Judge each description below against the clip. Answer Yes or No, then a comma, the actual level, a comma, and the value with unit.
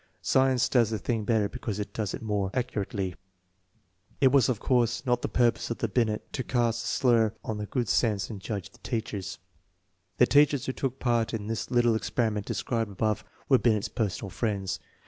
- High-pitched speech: No, low, 115 Hz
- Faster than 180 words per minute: Yes, average, 190 wpm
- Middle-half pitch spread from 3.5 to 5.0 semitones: No, average, 2.8 semitones